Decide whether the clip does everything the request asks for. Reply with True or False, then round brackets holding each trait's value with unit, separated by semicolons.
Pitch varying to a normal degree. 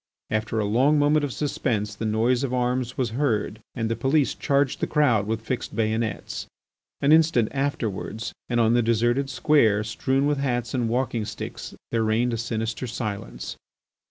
True (3.5 semitones)